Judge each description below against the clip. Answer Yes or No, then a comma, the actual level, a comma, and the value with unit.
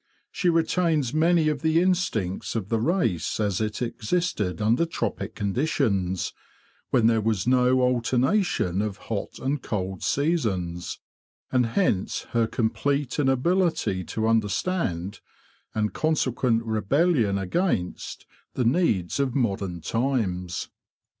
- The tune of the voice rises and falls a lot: Yes, wide, 7.0 semitones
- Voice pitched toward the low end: Yes, low, 115 Hz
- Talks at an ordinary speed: No, slow, 115 wpm